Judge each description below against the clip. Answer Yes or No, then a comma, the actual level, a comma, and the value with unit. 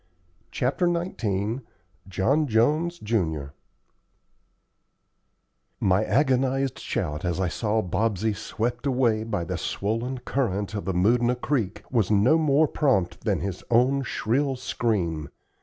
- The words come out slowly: Yes, slow, 120 wpm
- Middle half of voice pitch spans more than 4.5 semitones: Yes, average, 5.2 semitones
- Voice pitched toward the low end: Yes, low, 115 Hz